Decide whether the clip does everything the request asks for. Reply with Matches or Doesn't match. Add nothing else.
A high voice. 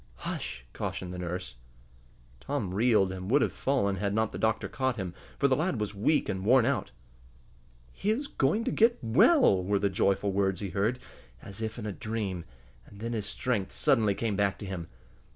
Doesn't match